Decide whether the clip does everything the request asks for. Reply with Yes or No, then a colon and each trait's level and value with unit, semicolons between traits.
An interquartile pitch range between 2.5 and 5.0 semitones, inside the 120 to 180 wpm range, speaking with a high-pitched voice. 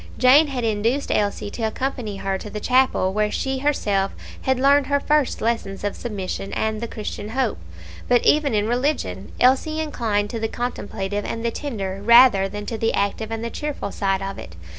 No: average, 4.3 semitones; average, 190 wpm; high, 225 Hz